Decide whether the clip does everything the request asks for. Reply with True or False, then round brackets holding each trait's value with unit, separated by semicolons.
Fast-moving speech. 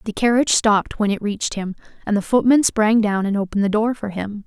True (240 wpm)